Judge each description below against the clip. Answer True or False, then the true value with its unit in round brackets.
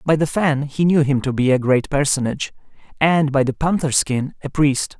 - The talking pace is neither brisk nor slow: False (215 wpm)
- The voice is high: False (145 Hz)